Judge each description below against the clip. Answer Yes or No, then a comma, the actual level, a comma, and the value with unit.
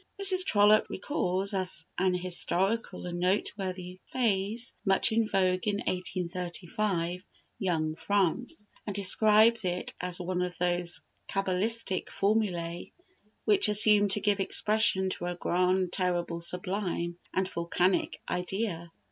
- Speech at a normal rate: No, slow, 120 wpm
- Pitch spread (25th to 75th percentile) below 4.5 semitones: Yes, average, 2.7 semitones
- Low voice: No, medium, 185 Hz